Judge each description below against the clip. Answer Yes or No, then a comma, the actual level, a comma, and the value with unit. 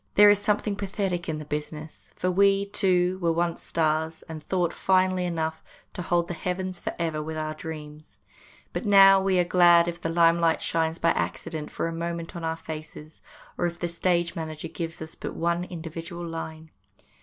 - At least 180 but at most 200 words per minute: Yes, average, 190 wpm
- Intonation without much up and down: Yes, narrow, 2.1 semitones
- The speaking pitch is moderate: Yes, medium, 170 Hz